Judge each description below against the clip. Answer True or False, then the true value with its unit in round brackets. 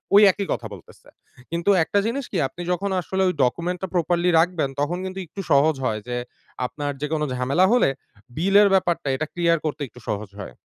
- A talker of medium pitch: True (170 Hz)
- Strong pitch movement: False (4.3 semitones)